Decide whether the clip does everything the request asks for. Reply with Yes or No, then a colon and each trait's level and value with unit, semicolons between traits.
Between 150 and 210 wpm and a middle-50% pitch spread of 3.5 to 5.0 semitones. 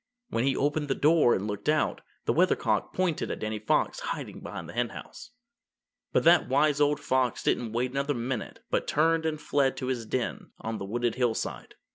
Yes: average, 190 wpm; average, 3.9 semitones